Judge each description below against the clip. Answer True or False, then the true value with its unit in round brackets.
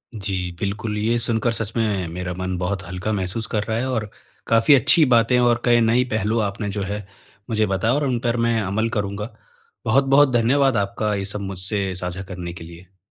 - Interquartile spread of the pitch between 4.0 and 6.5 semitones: False (3.3 semitones)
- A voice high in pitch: False (105 Hz)